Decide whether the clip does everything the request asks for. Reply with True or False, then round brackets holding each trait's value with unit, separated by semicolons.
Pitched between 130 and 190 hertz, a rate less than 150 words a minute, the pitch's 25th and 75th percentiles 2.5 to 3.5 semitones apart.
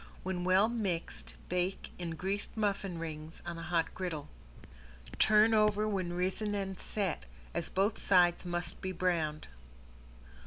True (185 Hz; 140 wpm; 2.8 semitones)